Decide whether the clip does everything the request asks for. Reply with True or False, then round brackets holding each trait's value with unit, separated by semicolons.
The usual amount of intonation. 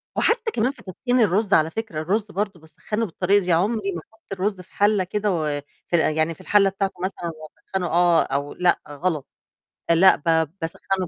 True (4.0 semitones)